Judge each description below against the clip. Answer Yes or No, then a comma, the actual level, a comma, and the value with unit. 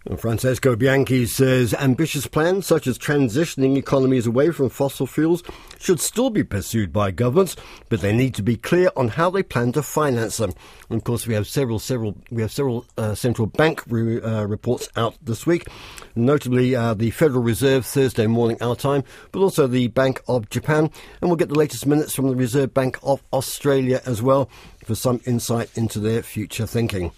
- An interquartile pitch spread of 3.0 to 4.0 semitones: Yes, average, 3.5 semitones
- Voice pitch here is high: No, low, 125 Hz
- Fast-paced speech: No, average, 195 wpm